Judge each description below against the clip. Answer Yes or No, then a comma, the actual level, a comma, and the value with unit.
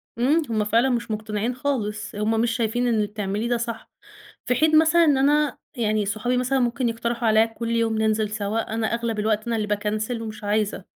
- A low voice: No, high, 225 Hz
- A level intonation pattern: Yes, narrow, 2.2 semitones